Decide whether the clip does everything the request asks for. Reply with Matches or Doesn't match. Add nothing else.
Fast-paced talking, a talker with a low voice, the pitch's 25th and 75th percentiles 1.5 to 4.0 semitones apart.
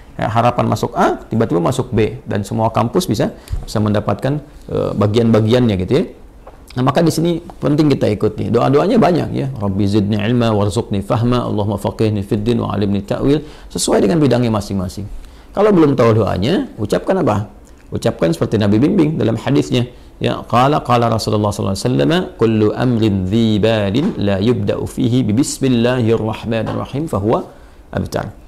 Matches